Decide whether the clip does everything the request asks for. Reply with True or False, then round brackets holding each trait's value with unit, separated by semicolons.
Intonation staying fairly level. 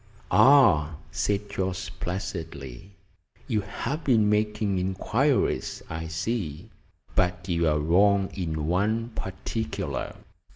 False (4.3 semitones)